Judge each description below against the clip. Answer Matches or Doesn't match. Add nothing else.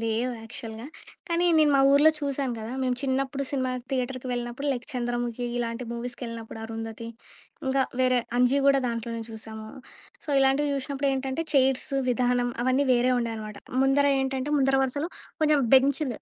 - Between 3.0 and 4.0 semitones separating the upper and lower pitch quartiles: Doesn't match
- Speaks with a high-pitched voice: Matches